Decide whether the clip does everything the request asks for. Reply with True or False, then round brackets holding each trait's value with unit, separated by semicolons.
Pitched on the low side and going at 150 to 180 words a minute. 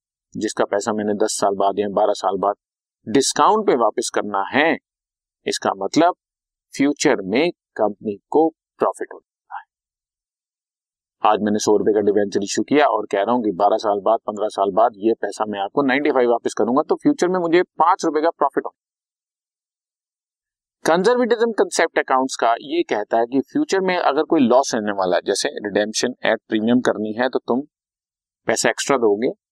True (120 Hz; 175 wpm)